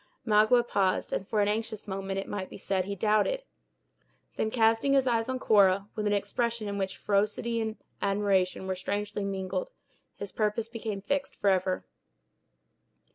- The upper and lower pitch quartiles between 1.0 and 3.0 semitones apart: Yes, narrow, 2.5 semitones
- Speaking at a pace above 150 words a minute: Yes, average, 160 wpm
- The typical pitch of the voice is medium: No, high, 210 Hz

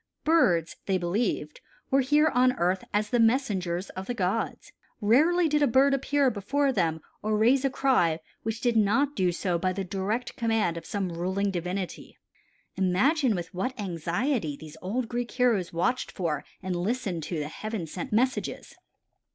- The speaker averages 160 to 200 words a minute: Yes, average, 165 wpm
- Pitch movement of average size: No, wide, 6.1 semitones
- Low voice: No, high, 210 Hz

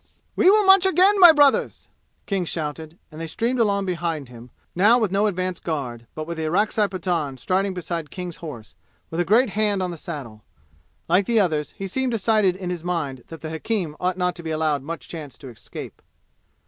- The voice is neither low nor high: Yes, medium, 180 Hz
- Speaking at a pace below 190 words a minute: No, average, 200 wpm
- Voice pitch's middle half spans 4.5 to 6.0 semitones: Yes, average, 4.8 semitones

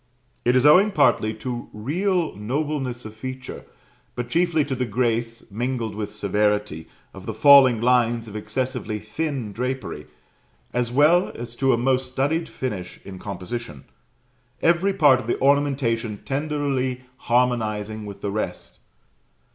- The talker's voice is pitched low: Yes, low, 125 Hz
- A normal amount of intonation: Yes, average, 4.3 semitones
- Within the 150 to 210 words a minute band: No, average, 140 wpm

